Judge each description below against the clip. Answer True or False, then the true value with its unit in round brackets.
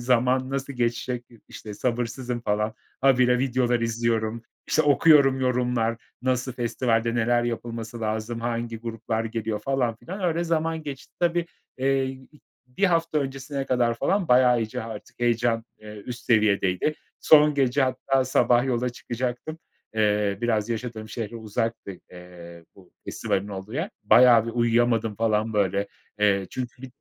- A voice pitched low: True (120 Hz)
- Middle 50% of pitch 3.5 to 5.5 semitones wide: False (2.8 semitones)